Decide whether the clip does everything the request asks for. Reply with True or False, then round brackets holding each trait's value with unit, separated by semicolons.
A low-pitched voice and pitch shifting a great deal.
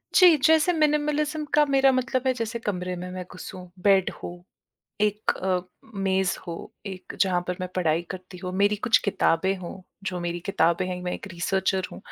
False (190 Hz; 5.9 semitones)